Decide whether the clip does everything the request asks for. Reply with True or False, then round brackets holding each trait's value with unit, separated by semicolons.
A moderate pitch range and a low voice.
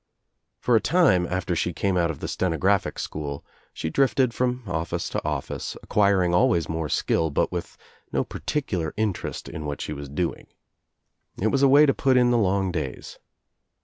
False (7.0 semitones; 95 Hz)